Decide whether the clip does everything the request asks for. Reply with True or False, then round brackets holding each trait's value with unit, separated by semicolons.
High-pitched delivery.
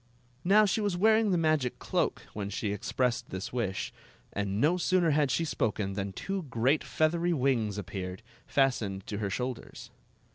False (130 Hz)